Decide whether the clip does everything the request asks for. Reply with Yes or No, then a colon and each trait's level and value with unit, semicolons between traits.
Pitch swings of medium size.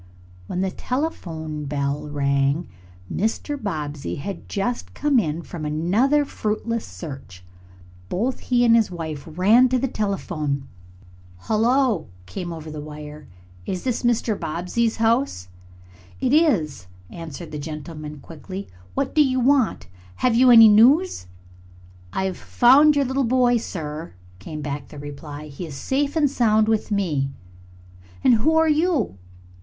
No: wide, 8.5 semitones